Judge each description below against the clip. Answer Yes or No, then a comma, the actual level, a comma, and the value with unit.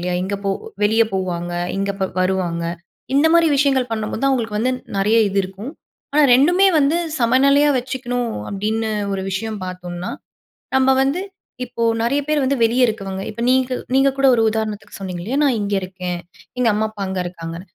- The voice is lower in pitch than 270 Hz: Yes, high, 220 Hz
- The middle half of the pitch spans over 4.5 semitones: Yes, wide, 5.4 semitones